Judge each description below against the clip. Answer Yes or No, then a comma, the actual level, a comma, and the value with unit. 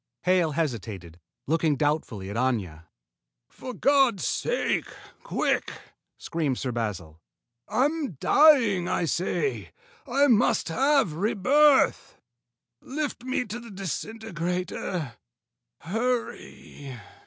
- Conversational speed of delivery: No, slow, 95 wpm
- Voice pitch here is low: No, medium, 180 Hz